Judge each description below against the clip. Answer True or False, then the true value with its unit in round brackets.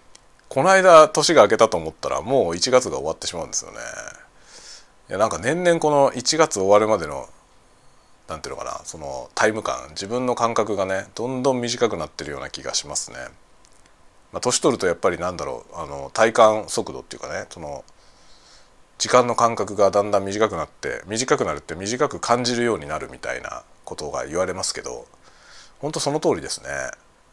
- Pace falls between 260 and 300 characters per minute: False (365 characters per minute)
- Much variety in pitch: False (4.2 semitones)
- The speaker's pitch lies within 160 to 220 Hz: False (115 Hz)